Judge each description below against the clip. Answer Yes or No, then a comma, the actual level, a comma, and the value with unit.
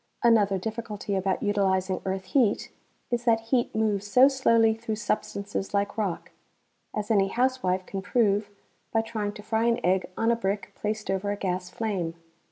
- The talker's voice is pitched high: Yes, high, 210 Hz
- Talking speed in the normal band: Yes, average, 170 wpm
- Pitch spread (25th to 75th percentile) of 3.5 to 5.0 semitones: No, average, 2.7 semitones